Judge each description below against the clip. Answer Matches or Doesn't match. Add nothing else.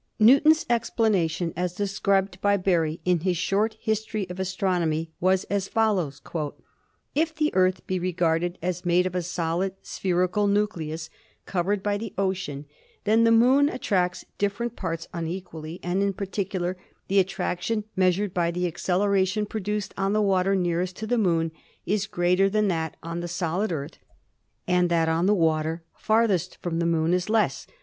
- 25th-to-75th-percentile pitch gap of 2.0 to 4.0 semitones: Matches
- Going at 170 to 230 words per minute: Doesn't match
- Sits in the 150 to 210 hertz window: Matches